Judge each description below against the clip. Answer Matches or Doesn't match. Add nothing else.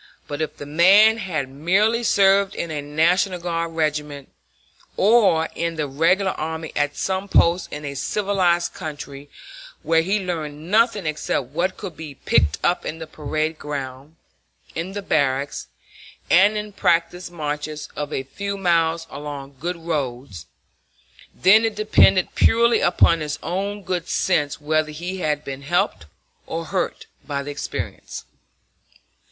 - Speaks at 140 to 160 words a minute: Matches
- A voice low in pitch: Doesn't match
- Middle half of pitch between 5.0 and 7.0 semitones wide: Doesn't match